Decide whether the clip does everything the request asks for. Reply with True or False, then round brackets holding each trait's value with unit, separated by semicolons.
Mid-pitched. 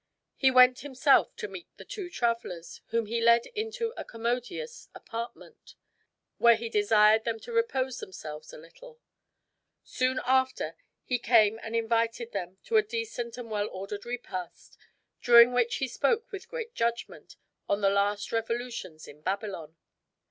False (235 Hz)